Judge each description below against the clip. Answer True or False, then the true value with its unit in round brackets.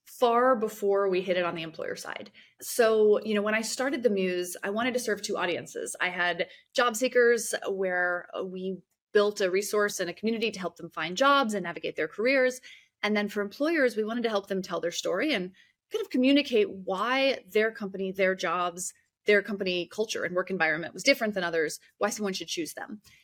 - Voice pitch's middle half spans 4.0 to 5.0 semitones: True (4.4 semitones)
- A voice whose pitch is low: False (205 Hz)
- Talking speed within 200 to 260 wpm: True (205 wpm)